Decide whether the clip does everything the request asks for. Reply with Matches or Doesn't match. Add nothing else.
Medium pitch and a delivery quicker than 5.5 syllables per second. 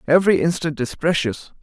Matches